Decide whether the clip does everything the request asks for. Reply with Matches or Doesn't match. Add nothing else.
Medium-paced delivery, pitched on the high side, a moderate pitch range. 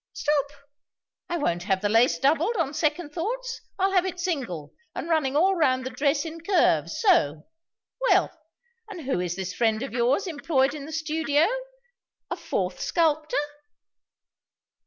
Matches